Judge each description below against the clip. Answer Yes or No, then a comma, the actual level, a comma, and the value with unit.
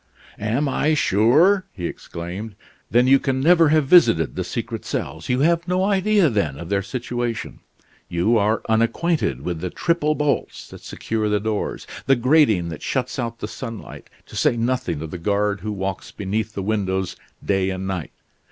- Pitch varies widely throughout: Yes, wide, 6.5 semitones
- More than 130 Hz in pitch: No, low, 110 Hz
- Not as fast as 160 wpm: No, average, 175 wpm